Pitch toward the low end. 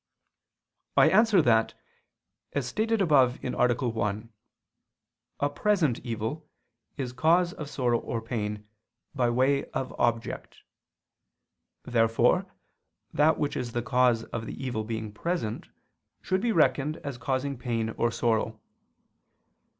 Yes: low, 125 Hz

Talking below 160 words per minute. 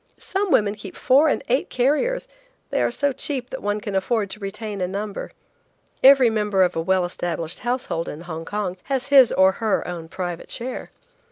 No: average, 190 wpm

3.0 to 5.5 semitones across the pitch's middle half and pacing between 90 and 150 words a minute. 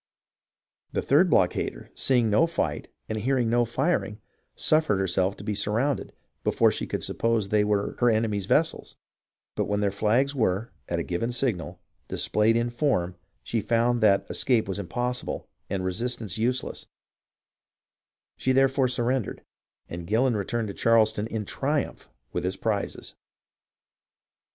Yes: average, 3.5 semitones; average, 145 wpm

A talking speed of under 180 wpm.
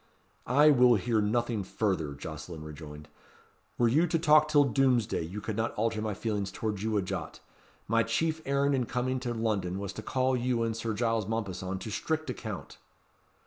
No: average, 185 wpm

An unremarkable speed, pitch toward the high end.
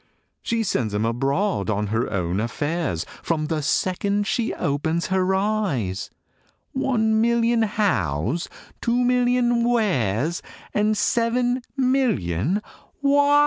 No: slow, 110 wpm; high, 195 Hz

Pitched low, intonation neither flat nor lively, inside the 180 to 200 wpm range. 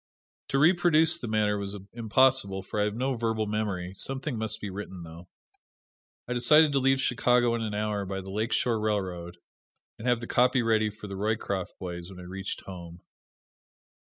Yes: low, 110 Hz; average, 4.1 semitones; average, 185 wpm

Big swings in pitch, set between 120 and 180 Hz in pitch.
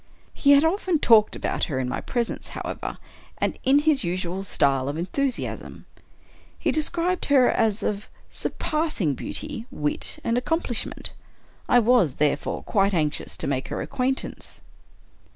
No: wide, 8.8 semitones; high, 230 Hz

